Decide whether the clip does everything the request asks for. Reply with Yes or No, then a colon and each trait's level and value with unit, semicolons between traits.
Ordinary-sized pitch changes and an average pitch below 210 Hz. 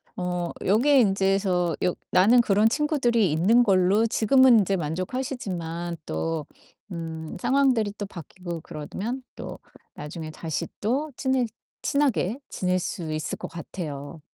No: wide, 6.1 semitones; high, 190 Hz